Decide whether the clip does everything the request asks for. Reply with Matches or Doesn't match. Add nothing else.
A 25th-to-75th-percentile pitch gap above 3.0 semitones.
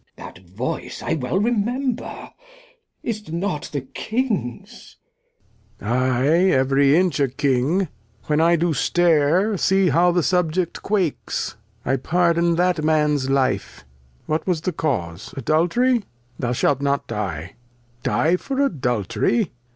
Matches